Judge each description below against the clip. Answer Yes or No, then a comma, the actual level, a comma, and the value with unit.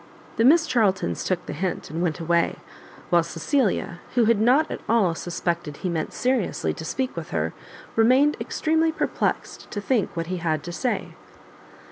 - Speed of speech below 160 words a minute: No, average, 170 wpm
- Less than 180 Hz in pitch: No, high, 190 Hz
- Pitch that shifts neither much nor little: No, wide, 7.0 semitones